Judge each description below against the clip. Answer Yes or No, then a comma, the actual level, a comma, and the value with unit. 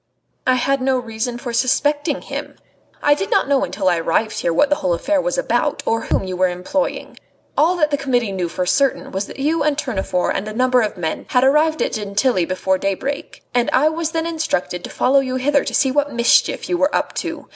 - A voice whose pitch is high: Yes, very high, 255 Hz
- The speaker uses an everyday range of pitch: No, wide, 6.6 semitones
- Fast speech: Yes, fast, 225 wpm